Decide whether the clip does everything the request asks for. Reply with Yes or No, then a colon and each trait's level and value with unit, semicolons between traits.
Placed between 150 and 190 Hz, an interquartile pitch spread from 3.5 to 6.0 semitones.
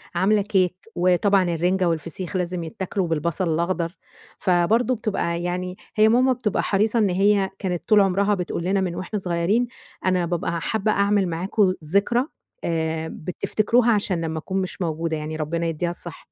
No: medium, 185 Hz; average, 3.1 semitones